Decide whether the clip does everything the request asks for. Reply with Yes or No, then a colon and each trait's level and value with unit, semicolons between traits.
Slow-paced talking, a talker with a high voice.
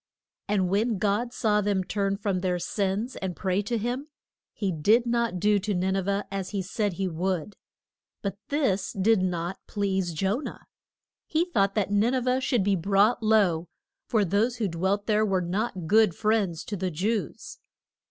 No: average, 180 wpm; high, 200 Hz